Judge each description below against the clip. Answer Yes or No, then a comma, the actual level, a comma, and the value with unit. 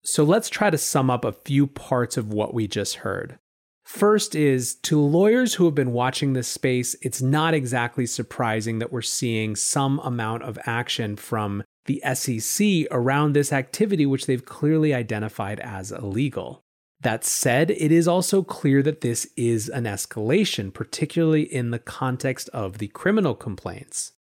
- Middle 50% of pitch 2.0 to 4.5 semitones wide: No, average, 4.9 semitones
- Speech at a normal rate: Yes, average, 165 wpm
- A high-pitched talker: No, low, 130 Hz